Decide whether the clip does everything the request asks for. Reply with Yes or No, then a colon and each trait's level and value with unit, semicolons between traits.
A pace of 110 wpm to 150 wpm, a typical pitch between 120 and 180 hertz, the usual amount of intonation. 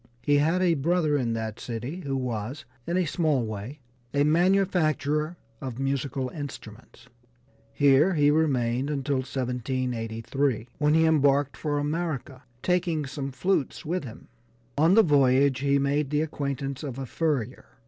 Yes: average, 145 wpm; medium, 140 Hz; average, 3.2 semitones